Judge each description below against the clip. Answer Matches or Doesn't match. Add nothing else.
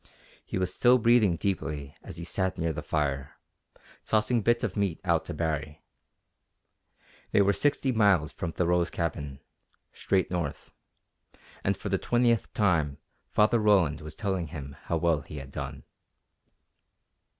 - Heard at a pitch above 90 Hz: Doesn't match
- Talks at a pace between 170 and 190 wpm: Doesn't match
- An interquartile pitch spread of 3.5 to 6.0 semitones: Matches